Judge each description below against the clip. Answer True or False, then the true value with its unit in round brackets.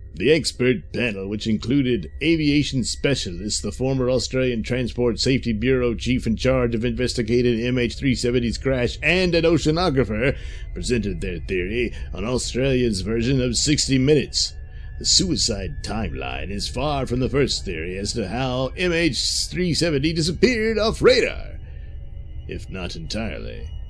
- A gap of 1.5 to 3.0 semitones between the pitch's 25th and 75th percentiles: False (4.3 semitones)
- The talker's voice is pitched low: True (125 Hz)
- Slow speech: True (130 wpm)